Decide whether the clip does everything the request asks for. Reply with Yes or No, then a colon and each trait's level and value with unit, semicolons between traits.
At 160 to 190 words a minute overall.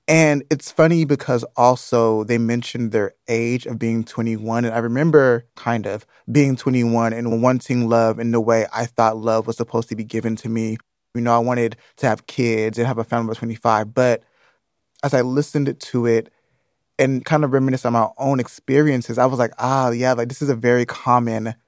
No: average, 200 wpm